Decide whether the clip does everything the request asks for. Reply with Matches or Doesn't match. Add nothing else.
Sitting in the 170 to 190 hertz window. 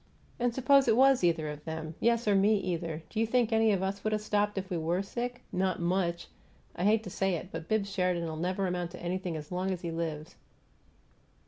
Matches